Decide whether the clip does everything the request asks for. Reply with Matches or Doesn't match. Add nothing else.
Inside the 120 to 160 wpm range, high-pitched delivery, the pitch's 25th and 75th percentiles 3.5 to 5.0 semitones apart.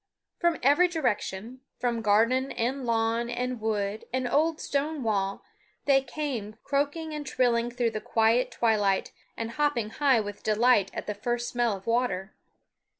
Matches